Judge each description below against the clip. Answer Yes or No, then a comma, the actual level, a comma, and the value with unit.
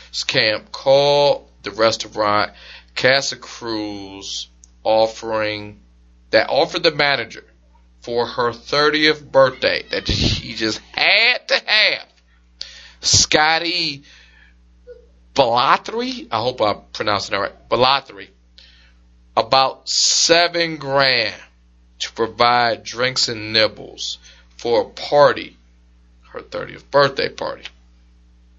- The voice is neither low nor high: No, low, 105 Hz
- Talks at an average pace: No, slow, 95 wpm